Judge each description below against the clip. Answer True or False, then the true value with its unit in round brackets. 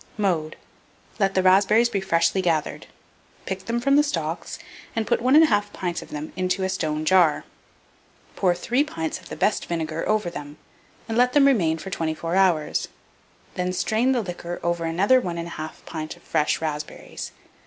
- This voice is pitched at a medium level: True (180 Hz)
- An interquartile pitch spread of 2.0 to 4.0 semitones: False (4.6 semitones)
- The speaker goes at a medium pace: True (175 wpm)